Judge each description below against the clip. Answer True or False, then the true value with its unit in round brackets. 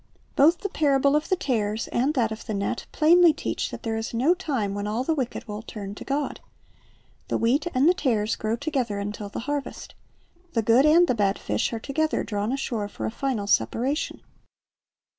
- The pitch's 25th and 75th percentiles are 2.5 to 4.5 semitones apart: False (5.4 semitones)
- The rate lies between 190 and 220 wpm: True (200 wpm)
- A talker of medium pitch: False (245 Hz)